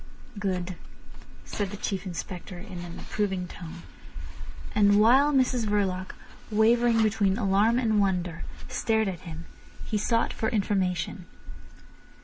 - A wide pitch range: No, average, 3.3 semitones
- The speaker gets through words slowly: Yes, slow, 125 wpm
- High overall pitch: Yes, high, 200 Hz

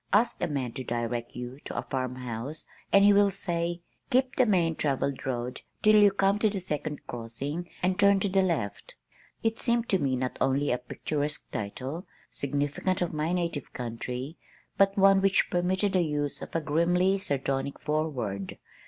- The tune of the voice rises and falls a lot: Yes, wide, 6.7 semitones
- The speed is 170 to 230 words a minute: Yes, average, 175 wpm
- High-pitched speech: No, medium, 155 Hz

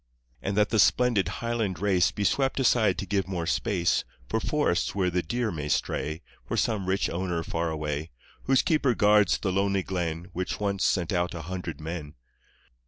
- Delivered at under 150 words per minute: No, average, 180 wpm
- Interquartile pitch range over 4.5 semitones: No, average, 3.7 semitones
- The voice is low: Yes, very low, 95 Hz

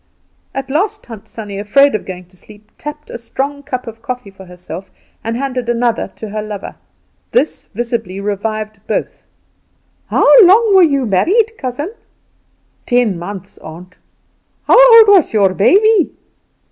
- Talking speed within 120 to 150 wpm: Yes, average, 145 wpm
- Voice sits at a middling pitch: No, high, 235 Hz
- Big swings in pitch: Yes, wide, 6.3 semitones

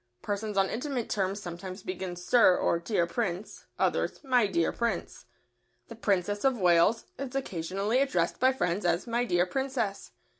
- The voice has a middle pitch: No, high, 200 Hz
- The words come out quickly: No, average, 155 wpm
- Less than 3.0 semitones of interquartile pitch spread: No, average, 5.0 semitones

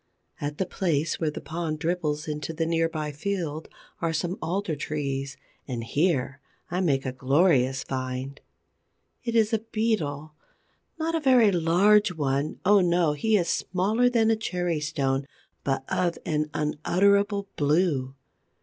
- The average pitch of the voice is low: No, medium, 160 Hz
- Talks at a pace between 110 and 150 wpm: Yes, average, 145 wpm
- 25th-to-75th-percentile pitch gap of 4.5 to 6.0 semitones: Yes, average, 4.8 semitones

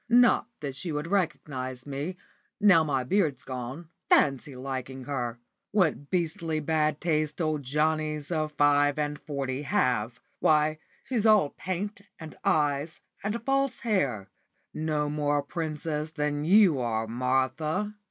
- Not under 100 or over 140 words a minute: Yes, slow, 135 wpm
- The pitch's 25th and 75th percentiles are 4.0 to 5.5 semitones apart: No, average, 3.5 semitones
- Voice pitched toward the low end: No, medium, 150 Hz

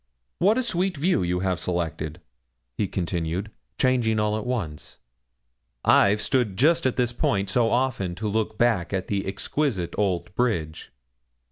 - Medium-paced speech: Yes, average, 150 wpm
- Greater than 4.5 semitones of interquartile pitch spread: Yes, wide, 5.6 semitones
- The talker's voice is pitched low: Yes, low, 105 Hz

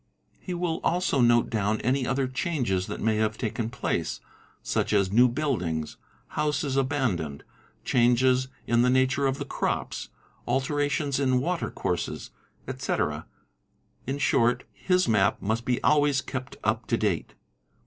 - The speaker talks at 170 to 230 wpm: No, average, 150 wpm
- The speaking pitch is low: Yes, low, 125 Hz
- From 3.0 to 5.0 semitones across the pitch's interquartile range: Yes, average, 4.3 semitones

